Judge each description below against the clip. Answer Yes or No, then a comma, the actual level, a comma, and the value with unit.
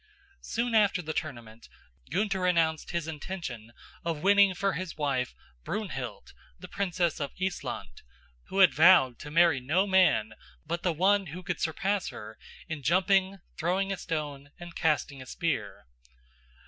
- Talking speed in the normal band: Yes, average, 150 wpm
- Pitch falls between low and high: Yes, medium, 170 Hz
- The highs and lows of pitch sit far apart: No, average, 4.5 semitones